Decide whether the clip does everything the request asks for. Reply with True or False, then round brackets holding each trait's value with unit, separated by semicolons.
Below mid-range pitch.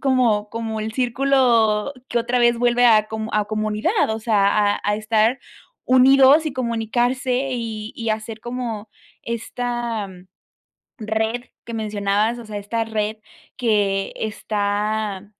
False (225 Hz)